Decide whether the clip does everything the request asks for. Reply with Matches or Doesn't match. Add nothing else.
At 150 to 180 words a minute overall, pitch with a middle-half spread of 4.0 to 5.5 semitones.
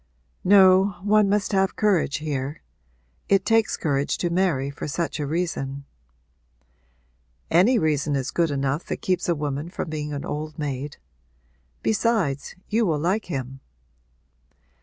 Doesn't match